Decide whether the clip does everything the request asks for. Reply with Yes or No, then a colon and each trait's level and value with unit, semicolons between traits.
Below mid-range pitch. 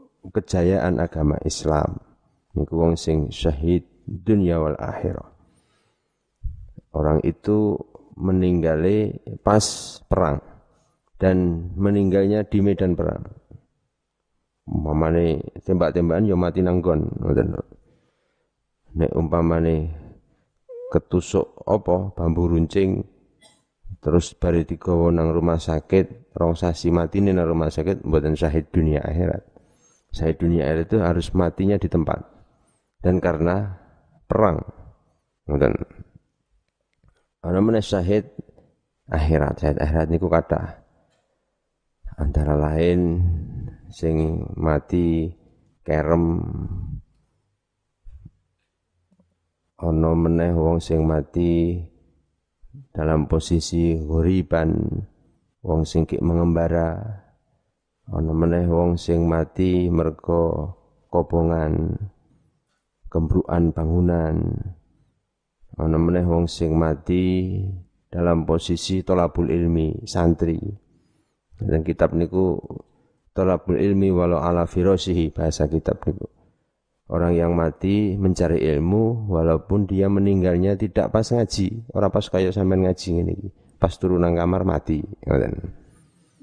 Yes: very low, 85 Hz